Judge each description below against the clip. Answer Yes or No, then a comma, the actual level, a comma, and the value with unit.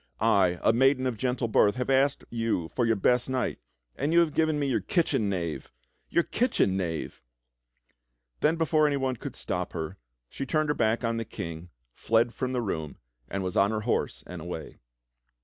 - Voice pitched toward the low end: Yes, low, 115 Hz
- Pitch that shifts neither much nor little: No, wide, 5.9 semitones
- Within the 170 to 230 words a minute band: Yes, average, 190 wpm